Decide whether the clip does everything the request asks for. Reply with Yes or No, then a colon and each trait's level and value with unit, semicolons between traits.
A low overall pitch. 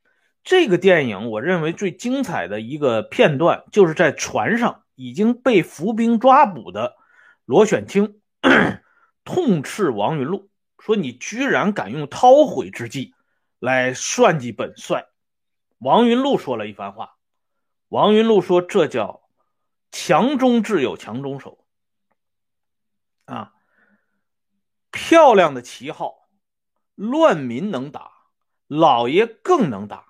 No: high, 205 Hz